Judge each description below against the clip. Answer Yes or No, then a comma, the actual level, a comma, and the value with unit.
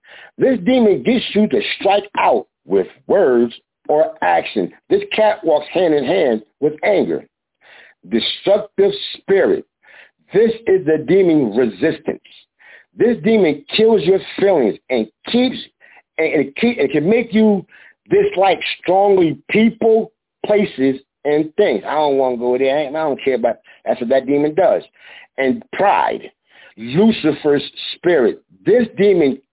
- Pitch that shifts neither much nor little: No, wide, 7.3 semitones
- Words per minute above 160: No, slow, 135 wpm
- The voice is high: Yes, high, 195 Hz